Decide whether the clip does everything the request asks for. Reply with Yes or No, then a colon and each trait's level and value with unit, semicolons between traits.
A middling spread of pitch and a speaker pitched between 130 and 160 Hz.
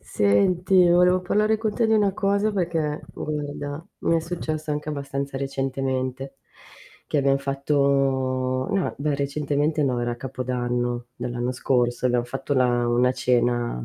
Yes: average, 3.9 semitones; medium, 140 Hz